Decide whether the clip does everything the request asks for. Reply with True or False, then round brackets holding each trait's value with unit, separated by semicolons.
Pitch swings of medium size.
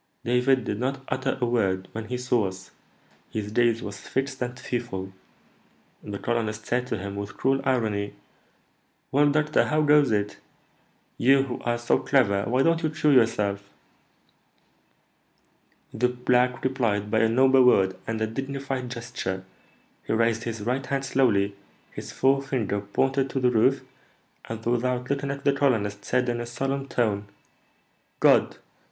True (3.8 semitones)